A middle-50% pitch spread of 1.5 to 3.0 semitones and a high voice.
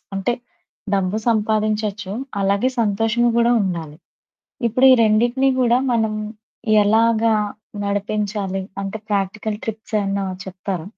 Yes: narrow, 2.4 semitones; high, 215 Hz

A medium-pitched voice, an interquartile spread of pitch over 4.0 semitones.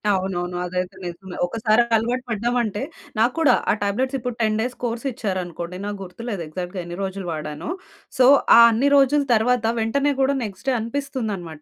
No: high, 220 Hz; wide, 5.4 semitones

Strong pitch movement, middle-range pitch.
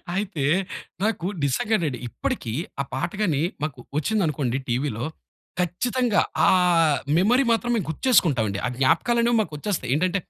Yes: wide, 8.0 semitones; medium, 170 Hz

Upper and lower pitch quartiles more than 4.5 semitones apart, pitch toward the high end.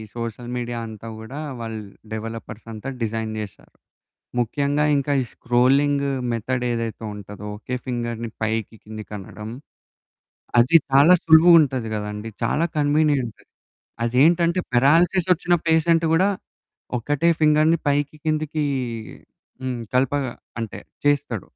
No: average, 5.0 semitones; low, 125 Hz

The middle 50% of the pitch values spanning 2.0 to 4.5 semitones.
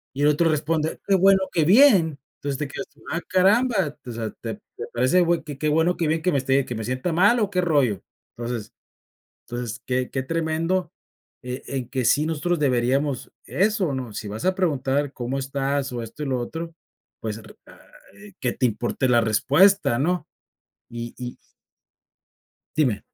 No: average, 5.2 semitones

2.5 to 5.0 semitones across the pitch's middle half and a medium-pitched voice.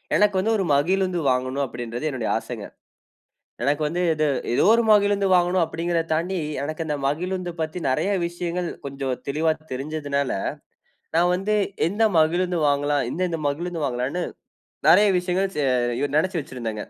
Yes: average, 4.4 semitones; medium, 165 Hz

